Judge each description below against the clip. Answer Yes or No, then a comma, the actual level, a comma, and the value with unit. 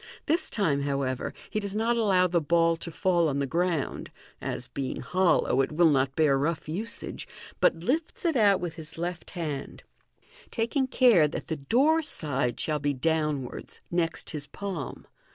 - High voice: No, medium, 165 Hz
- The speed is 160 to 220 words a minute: Yes, average, 175 wpm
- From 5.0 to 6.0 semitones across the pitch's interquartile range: Yes, wide, 5.5 semitones